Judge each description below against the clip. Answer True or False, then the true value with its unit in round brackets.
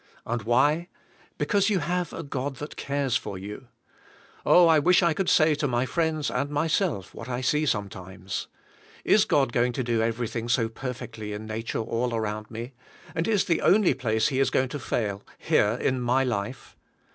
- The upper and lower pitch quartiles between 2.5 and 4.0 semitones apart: False (5.3 semitones)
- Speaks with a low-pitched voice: True (125 Hz)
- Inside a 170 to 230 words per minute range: True (185 wpm)